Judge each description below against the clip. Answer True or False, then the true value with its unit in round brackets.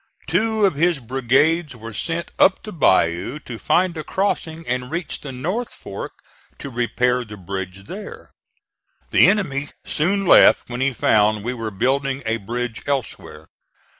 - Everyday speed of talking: True (155 wpm)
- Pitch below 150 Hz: True (135 Hz)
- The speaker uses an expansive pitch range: True (6.8 semitones)